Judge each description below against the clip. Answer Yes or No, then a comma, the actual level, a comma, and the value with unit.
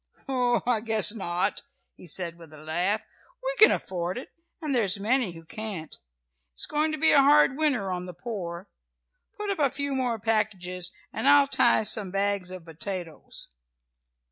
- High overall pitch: Yes, high, 210 Hz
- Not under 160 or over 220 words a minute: Yes, average, 175 wpm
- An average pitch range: No, wide, 6.7 semitones